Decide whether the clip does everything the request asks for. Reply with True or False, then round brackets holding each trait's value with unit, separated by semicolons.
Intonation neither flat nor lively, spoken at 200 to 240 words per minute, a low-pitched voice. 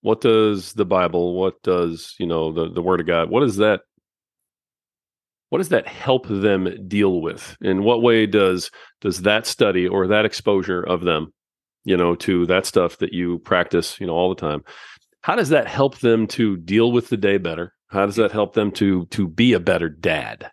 True (3.4 semitones; 205 wpm; 95 Hz)